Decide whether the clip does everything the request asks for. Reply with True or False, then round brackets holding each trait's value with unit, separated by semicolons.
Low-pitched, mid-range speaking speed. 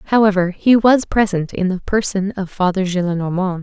False (195 Hz; 165 wpm)